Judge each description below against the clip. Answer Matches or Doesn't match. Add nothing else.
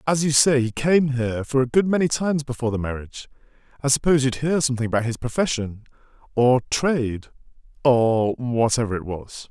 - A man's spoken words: Matches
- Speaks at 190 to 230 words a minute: Doesn't match